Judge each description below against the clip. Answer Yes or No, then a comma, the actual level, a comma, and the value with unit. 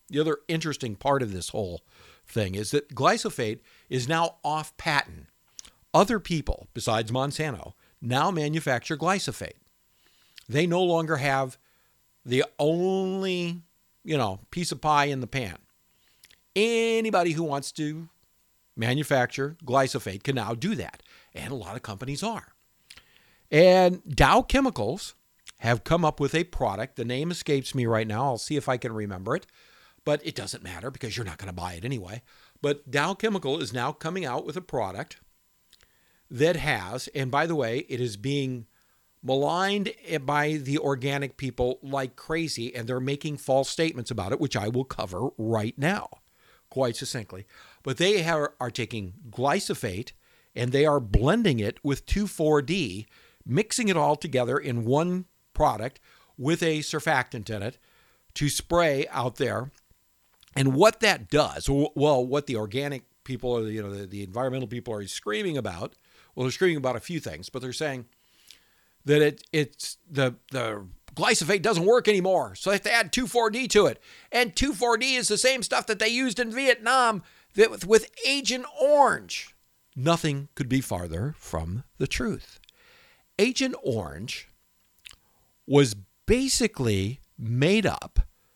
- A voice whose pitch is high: No, medium, 140 Hz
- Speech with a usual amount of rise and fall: No, wide, 6.0 semitones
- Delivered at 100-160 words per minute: Yes, average, 155 wpm